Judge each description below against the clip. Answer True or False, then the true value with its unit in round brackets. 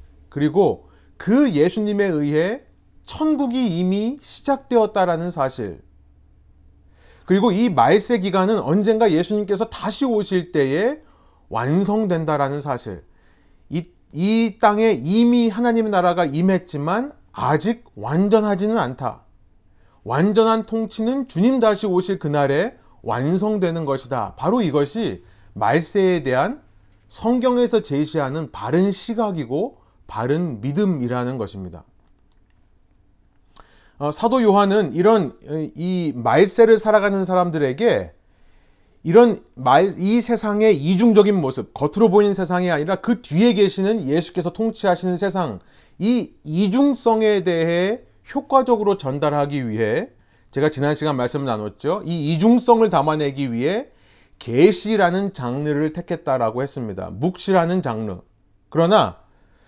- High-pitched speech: False (175 Hz)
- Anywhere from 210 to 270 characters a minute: True (265 characters per minute)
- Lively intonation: True (8.1 semitones)